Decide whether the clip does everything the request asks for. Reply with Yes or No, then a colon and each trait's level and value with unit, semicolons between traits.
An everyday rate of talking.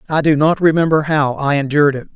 No: fast, 220 wpm